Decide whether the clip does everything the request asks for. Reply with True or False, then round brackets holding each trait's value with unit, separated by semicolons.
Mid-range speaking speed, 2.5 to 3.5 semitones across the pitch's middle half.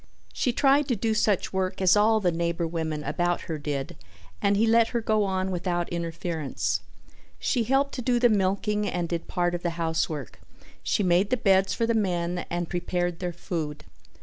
False (190 wpm; 4.1 semitones)